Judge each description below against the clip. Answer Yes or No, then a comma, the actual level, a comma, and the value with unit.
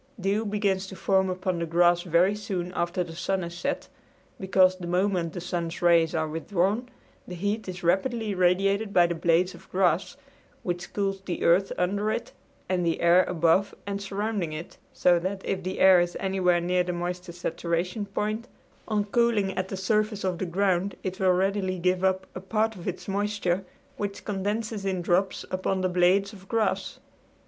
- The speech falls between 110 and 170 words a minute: No, average, 185 wpm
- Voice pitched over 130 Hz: Yes, medium, 185 Hz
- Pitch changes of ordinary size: No, narrow, 2.2 semitones